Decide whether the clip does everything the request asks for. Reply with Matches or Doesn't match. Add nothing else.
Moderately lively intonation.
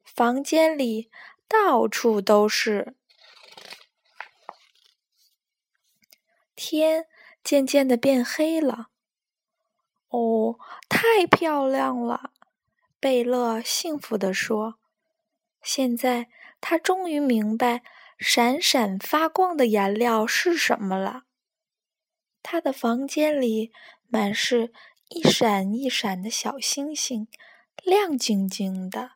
Doesn't match